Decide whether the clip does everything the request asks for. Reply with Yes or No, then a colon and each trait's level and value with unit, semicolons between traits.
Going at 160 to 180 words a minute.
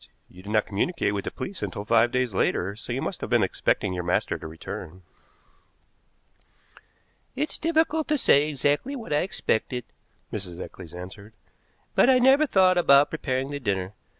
Yes: average, 170 wpm